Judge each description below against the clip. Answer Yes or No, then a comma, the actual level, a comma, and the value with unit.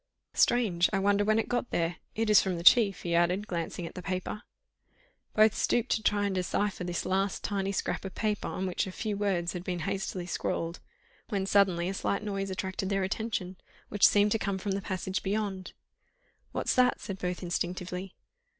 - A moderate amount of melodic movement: No, narrow, 2.2 semitones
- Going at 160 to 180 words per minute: No, average, 190 wpm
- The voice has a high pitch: Yes, high, 195 Hz